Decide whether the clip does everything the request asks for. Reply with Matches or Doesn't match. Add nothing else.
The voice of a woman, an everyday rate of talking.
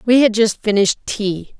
Matches